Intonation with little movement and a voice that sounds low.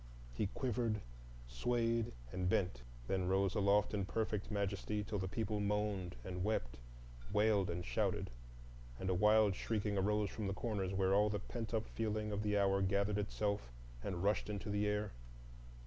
Yes: narrow, 1.7 semitones; low, 105 Hz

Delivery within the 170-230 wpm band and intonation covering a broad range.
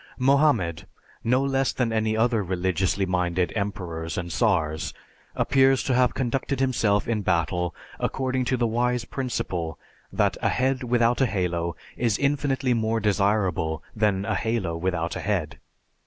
No: average, 145 wpm; wide, 5.9 semitones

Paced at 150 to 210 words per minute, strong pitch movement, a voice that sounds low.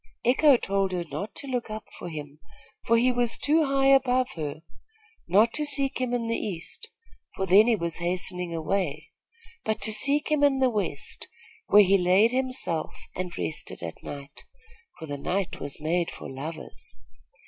No: average, 175 wpm; wide, 7.2 semitones; high, 200 Hz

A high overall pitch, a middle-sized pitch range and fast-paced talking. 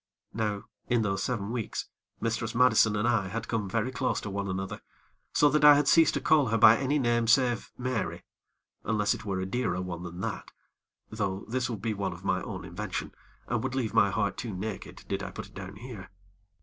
No: low, 110 Hz; average, 3.6 semitones; fast, 215 wpm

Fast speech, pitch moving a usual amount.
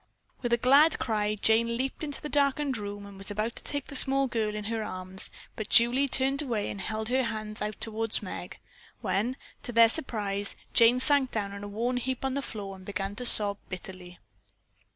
Yes: fast, 210 wpm; average, 4.1 semitones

